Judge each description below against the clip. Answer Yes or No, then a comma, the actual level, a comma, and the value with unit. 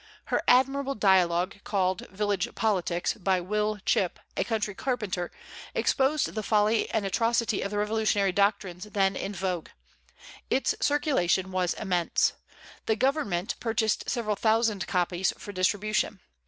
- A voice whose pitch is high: Yes, high, 205 Hz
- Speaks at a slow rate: Yes, slow, 130 wpm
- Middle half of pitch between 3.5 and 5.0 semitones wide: No, average, 3.1 semitones